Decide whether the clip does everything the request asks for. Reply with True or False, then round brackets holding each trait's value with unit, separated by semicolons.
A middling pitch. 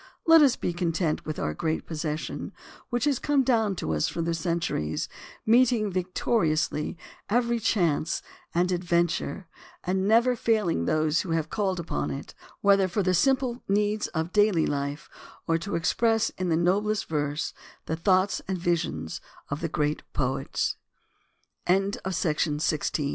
True (180 Hz)